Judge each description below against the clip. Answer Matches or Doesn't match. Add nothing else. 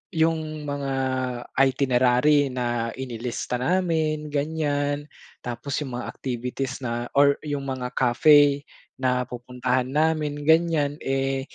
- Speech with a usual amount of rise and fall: Matches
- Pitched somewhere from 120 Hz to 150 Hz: Matches